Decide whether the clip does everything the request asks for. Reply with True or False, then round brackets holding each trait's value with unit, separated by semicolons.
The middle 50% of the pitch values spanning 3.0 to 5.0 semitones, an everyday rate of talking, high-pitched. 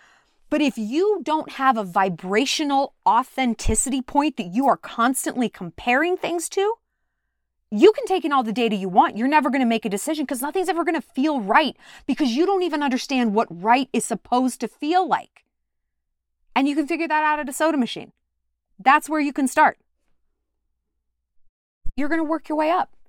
False (5.4 semitones; 190 wpm; 275 Hz)